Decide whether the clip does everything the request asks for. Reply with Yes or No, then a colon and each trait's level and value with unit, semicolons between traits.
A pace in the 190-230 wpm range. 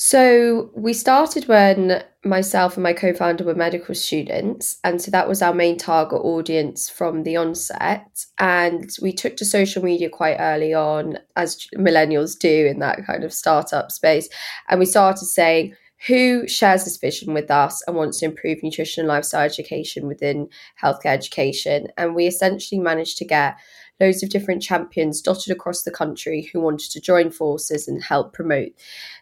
No: average, 170 wpm